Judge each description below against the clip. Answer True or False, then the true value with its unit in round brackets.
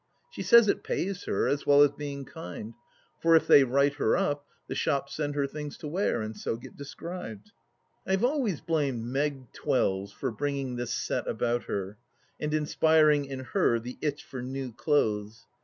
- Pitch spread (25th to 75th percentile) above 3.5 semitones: True (4.0 semitones)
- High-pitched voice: False (140 Hz)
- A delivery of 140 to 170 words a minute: False (185 wpm)